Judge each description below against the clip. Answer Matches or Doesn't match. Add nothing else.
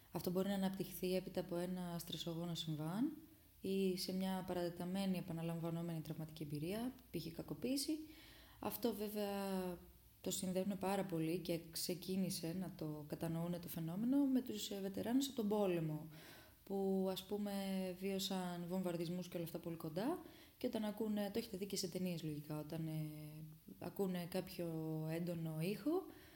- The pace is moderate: Matches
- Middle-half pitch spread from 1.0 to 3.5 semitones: Matches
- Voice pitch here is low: Doesn't match